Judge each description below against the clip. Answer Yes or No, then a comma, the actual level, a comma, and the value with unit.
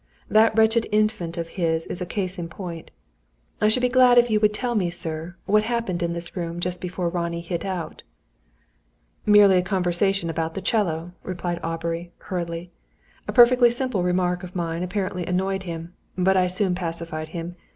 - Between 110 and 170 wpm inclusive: No, average, 180 wpm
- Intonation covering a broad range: No, average, 3.4 semitones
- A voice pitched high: No, medium, 180 Hz